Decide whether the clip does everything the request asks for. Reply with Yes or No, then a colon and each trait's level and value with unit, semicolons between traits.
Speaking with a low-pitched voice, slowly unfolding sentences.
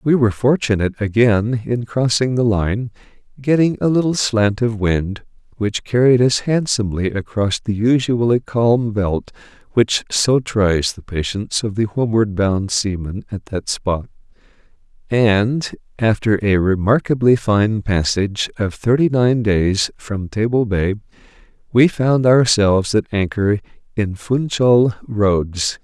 Yes: low, 110 Hz; slow, 130 wpm